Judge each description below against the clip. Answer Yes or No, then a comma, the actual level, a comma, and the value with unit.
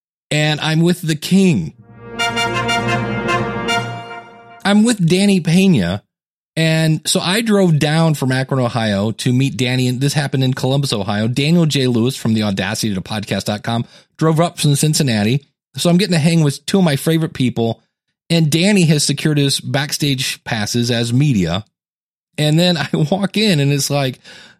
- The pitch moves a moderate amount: No, wide, 6.1 semitones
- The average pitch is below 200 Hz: Yes, medium, 140 Hz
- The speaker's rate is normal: Yes, average, 160 wpm